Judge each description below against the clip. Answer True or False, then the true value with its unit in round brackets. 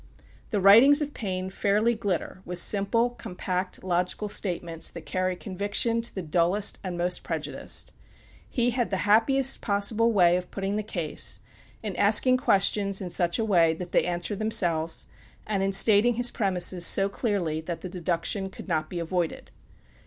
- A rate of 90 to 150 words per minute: False (165 wpm)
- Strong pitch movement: False (3.4 semitones)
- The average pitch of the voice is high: True (195 Hz)